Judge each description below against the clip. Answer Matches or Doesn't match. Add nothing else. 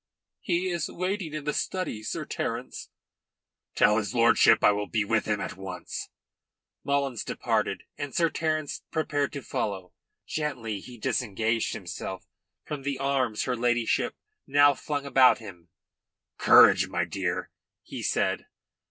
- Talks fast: Doesn't match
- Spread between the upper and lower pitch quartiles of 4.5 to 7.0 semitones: Matches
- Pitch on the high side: Doesn't match